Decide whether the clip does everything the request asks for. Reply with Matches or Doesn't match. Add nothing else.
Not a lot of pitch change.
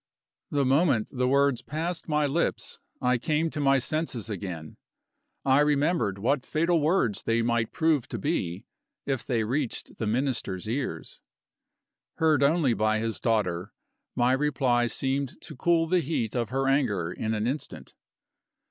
Doesn't match